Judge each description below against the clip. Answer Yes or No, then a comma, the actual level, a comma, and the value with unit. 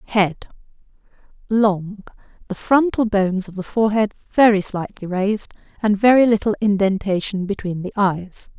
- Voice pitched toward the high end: Yes, high, 205 Hz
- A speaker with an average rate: No, slow, 120 wpm